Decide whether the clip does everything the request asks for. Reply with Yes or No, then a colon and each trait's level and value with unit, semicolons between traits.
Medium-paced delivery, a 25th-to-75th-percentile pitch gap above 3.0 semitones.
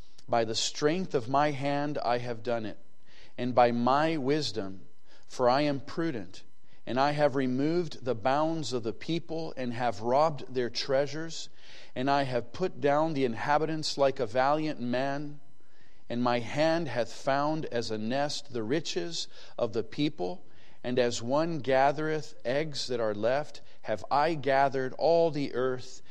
Yes: average, 160 wpm; average, 3.8 semitones